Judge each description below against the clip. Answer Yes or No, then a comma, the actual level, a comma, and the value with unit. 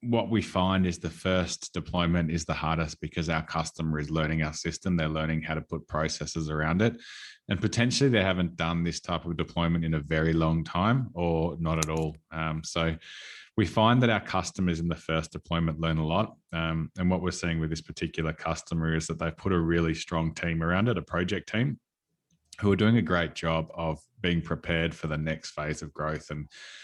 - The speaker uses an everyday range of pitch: No, narrow, 1.9 semitones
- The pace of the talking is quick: Yes, fast, 210 wpm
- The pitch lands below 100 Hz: Yes, very low, 80 Hz